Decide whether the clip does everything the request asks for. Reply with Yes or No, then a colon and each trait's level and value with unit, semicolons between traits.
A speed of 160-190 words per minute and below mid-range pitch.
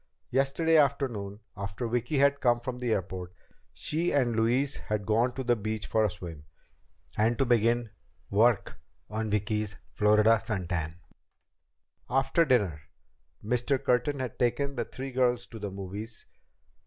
No: average, 145 wpm; low, 115 Hz